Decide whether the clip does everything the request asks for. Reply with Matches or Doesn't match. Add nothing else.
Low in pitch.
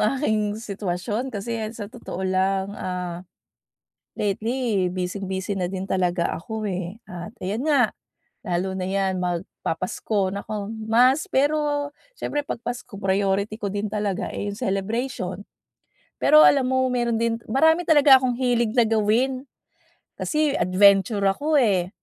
Doesn't match